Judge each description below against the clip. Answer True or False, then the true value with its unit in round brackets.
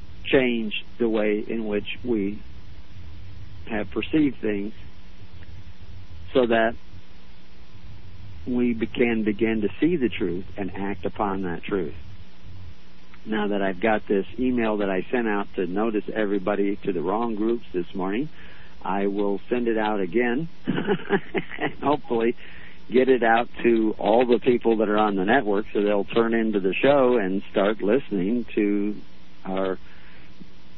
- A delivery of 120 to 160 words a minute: True (140 wpm)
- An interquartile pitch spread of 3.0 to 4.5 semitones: True (3.3 semitones)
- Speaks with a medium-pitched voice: False (100 Hz)